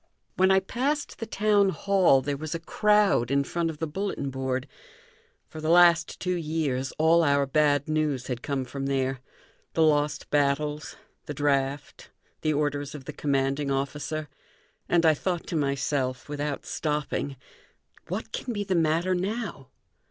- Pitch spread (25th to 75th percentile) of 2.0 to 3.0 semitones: No, average, 3.6 semitones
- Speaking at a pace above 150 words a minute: Yes, average, 160 wpm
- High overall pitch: No, medium, 150 Hz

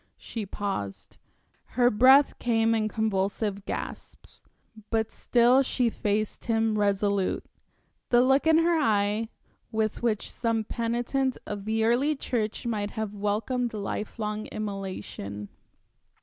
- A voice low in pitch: No, high, 220 Hz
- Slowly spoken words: Yes, slow, 120 wpm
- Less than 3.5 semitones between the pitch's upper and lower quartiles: Yes, average, 2.8 semitones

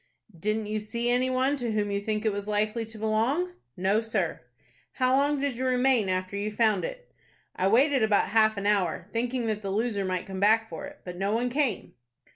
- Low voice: No, high, 220 Hz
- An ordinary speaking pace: No, fast, 215 wpm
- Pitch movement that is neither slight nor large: Yes, average, 3.5 semitones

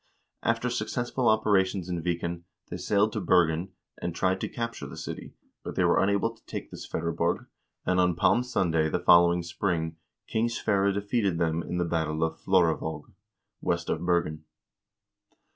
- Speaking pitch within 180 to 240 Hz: No, very low, 90 Hz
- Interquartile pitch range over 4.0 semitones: No, average, 3.4 semitones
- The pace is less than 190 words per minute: Yes, average, 160 wpm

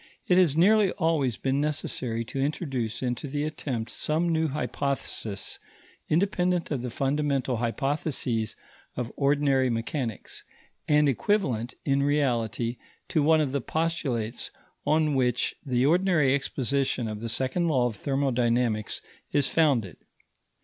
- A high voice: No, medium, 140 Hz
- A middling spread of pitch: Yes, average, 4.0 semitones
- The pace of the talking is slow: Yes, slow, 130 wpm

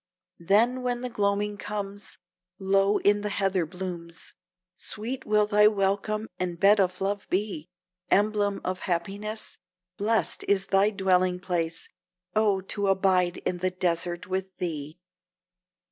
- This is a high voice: Yes, high, 195 Hz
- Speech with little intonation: Yes, narrow, 2.3 semitones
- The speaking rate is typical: No, slow, 130 wpm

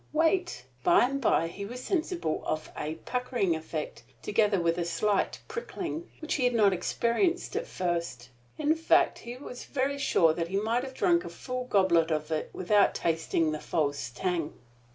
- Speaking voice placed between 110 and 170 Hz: No, high, 205 Hz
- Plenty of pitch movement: Yes, wide, 8.5 semitones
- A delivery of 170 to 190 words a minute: Yes, average, 175 wpm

